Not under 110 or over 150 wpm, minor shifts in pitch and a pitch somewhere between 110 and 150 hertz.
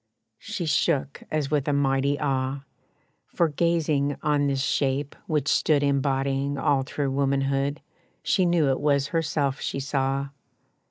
Yes: average, 140 wpm; narrow, 1.6 semitones; medium, 140 Hz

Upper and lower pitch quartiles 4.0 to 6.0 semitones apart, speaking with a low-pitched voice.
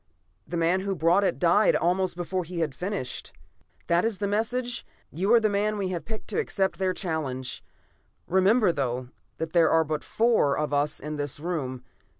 No: average, 4.8 semitones; medium, 175 Hz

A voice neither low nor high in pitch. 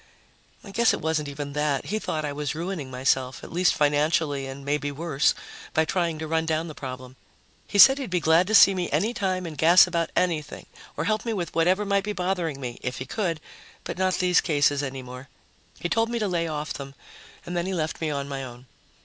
Yes: medium, 160 Hz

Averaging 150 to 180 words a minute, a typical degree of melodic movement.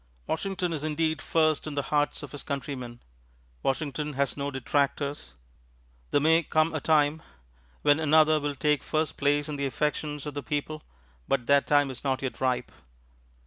No: average, 170 wpm; narrow, 1.7 semitones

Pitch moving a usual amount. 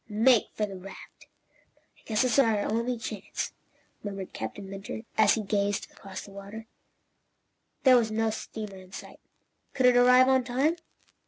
Yes: average, 3.6 semitones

